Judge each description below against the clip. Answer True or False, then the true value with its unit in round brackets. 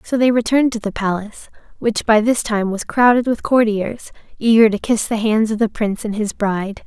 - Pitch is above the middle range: True (220 Hz)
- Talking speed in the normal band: False (220 wpm)